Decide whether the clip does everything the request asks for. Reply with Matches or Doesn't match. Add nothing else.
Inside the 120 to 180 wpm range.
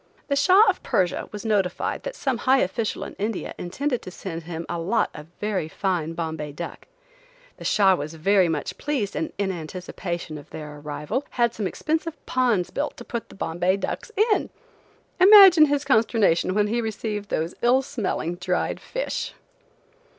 Matches